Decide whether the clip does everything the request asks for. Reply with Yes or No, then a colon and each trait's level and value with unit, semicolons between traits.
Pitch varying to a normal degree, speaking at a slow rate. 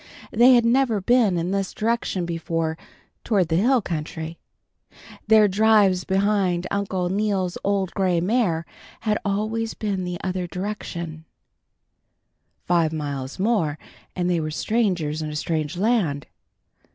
Yes: average, 4.2 semitones; slow, 130 wpm